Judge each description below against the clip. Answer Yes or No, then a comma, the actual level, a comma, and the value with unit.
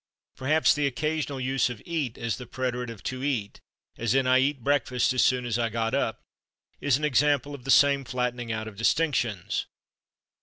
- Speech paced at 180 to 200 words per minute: Yes, average, 190 wpm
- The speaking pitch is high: No, low, 130 Hz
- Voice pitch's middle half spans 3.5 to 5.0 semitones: No, average, 3.0 semitones